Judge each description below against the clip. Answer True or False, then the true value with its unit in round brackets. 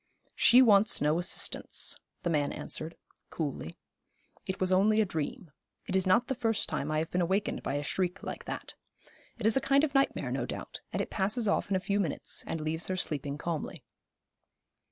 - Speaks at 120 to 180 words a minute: False (195 wpm)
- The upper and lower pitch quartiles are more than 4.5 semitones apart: True (5.4 semitones)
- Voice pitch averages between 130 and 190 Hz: True (185 Hz)